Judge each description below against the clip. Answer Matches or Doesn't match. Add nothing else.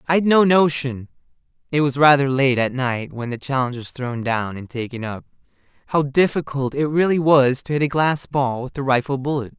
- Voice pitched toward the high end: Doesn't match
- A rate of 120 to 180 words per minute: Doesn't match